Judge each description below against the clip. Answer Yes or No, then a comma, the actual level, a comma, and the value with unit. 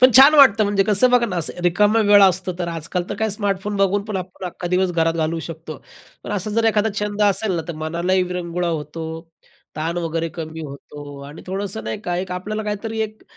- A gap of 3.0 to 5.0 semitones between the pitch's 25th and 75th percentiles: Yes, average, 3.8 semitones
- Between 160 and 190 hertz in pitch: Yes, medium, 185 Hz